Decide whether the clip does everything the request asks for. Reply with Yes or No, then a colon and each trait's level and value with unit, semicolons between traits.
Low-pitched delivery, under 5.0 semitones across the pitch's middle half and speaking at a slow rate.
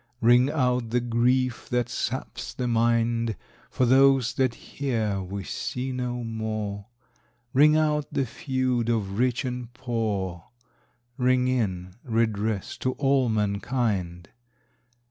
Yes: low, 120 Hz; average, 2.8 semitones; slow, 120 wpm